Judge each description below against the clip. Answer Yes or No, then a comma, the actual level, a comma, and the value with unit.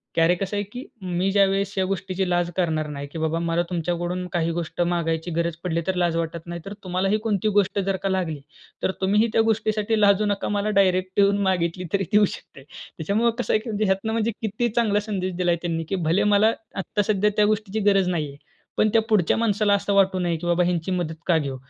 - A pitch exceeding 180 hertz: Yes, high, 190 Hz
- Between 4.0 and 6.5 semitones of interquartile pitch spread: No, average, 3.1 semitones